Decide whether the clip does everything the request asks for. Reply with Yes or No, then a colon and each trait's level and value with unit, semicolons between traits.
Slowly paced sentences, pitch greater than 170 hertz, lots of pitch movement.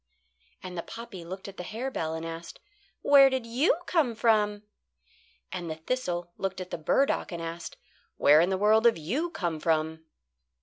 No: average, 175 wpm; high, 190 Hz; wide, 5.8 semitones